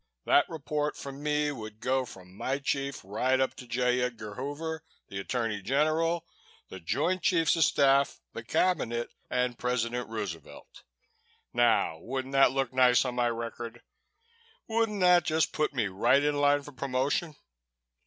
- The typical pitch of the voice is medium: No, low, 130 Hz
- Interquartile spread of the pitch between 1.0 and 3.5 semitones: No, average, 3.9 semitones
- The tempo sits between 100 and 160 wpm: Yes, average, 155 wpm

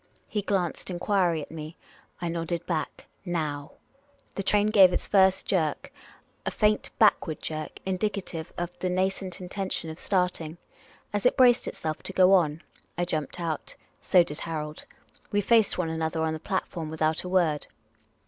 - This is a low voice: No, medium, 175 Hz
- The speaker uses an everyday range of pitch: Yes, average, 3.3 semitones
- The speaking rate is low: No, average, 165 wpm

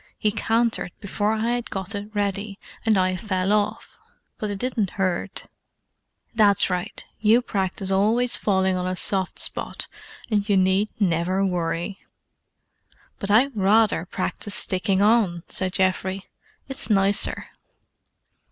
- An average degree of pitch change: No, narrow, 2.3 semitones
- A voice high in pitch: Yes, high, 200 Hz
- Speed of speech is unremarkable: No, slow, 130 wpm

